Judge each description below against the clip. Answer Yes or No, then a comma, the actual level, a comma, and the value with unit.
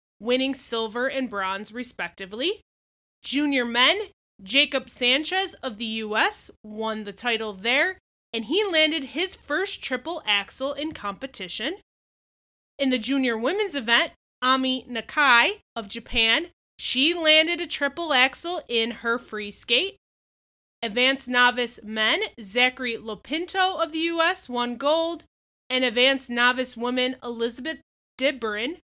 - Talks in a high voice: Yes, very high, 255 Hz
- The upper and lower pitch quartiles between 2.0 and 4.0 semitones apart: No, average, 5.2 semitones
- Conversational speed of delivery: No, slow, 125 wpm